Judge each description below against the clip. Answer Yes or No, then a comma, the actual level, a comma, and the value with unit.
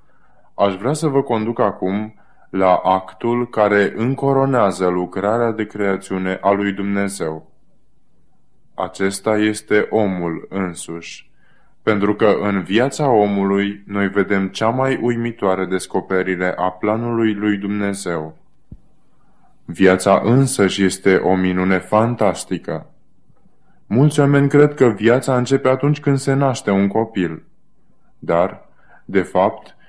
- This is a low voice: Yes, low, 100 Hz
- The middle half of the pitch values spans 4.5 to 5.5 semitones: No, average, 4.0 semitones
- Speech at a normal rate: No, slow, 110 wpm